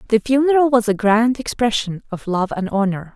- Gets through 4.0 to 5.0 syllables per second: No, 5.3 syllables/s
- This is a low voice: No, high, 225 Hz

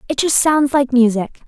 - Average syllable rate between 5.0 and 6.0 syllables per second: No, 4.8 syllables/s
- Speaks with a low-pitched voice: No, very high, 265 Hz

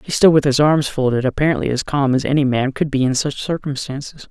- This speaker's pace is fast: Yes, fast, 235 wpm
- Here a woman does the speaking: No, male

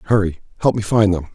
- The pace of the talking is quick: Yes, fast, 225 wpm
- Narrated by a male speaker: Yes, male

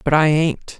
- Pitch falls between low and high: Yes, medium, 155 Hz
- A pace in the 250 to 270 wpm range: No, fast, 225 wpm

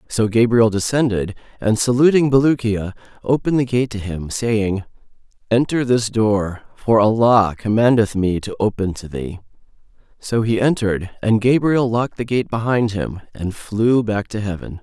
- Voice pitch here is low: Yes, low, 110 Hz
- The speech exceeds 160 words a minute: No, average, 155 wpm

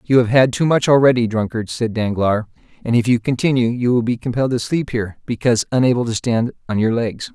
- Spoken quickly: Yes, fast, 220 wpm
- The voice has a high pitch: No, low, 120 Hz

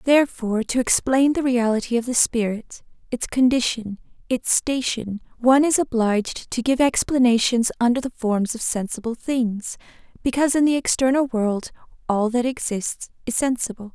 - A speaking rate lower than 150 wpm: Yes, average, 140 wpm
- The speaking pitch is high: Yes, high, 240 Hz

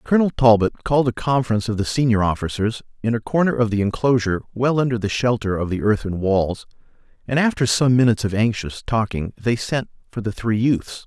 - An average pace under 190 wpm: No, average, 195 wpm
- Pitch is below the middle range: Yes, low, 115 Hz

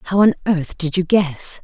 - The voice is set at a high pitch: No, medium, 175 Hz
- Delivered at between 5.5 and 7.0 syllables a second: No, 4.1 syllables/s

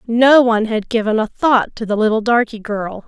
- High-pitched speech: Yes, high, 225 Hz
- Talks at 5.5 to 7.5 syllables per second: No, 5.2 syllables/s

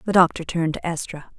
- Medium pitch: Yes, medium, 170 Hz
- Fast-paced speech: Yes, fast, 215 wpm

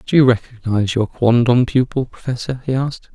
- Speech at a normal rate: Yes, average, 170 wpm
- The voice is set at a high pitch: No, low, 120 Hz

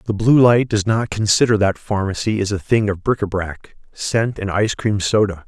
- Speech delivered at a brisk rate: Yes, fast, 220 wpm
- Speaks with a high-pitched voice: No, low, 105 Hz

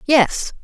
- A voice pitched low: No, very high, 260 Hz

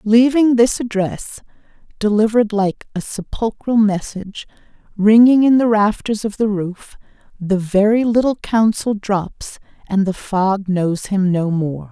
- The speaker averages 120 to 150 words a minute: Yes, slow, 135 wpm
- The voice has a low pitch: No, high, 210 Hz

